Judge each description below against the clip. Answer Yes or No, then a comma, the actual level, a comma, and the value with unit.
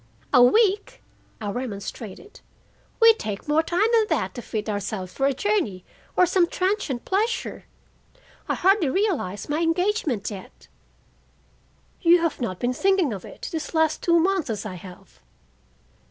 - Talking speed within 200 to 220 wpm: No, average, 155 wpm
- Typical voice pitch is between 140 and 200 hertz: No, very high, 310 Hz